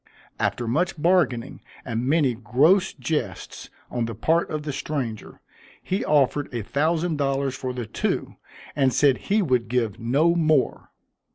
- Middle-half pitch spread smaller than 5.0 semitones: Yes, average, 4.4 semitones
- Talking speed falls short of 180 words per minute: Yes, average, 150 wpm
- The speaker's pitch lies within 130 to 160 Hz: Yes, medium, 140 Hz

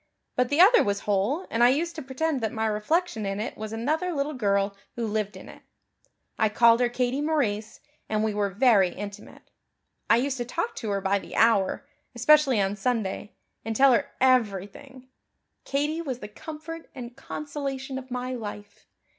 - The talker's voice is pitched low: No, high, 245 Hz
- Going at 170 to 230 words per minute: Yes, average, 180 wpm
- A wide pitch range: No, average, 5.0 semitones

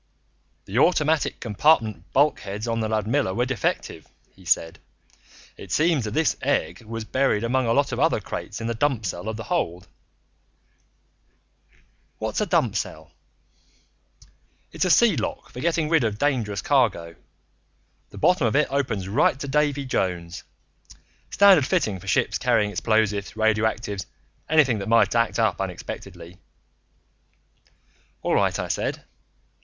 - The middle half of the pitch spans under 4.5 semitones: No, wide, 5.6 semitones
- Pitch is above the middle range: No, low, 115 Hz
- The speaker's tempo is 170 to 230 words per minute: No, average, 145 wpm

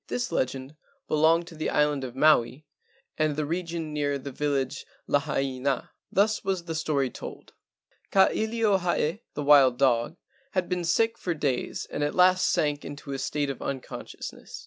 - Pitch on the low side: No, medium, 150 Hz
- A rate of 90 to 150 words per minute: No, average, 170 wpm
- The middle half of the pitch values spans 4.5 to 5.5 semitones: No, average, 3.9 semitones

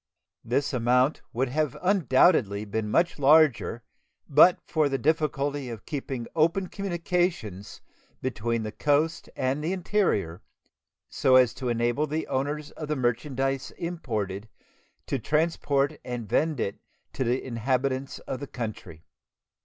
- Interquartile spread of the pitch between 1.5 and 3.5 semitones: No, average, 4.6 semitones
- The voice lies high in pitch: No, low, 135 Hz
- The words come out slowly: Yes, slow, 130 wpm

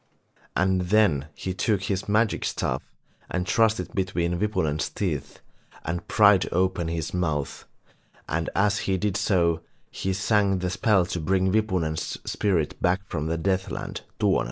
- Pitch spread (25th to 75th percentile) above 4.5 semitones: No, average, 3.0 semitones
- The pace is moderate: Yes, average, 150 wpm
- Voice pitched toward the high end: No, very low, 95 Hz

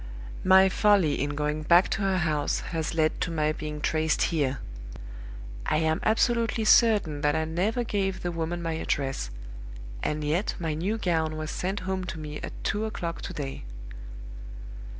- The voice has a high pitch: No, medium, 165 Hz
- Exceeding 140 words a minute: Yes, average, 170 wpm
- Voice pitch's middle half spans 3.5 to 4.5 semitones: Yes, average, 3.8 semitones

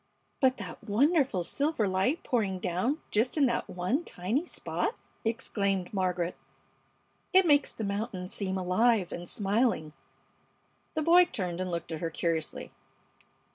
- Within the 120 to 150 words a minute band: Yes, slow, 135 wpm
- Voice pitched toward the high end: Yes, high, 200 Hz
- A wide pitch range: Yes, wide, 6.2 semitones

